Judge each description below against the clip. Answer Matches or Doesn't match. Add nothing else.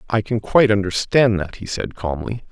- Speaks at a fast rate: Doesn't match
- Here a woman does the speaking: Doesn't match